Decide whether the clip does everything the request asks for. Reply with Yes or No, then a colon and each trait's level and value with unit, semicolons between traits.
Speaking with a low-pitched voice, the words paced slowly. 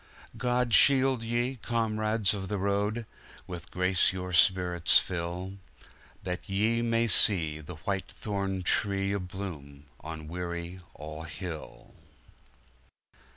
Yes: very low, 95 Hz; slow, 115 wpm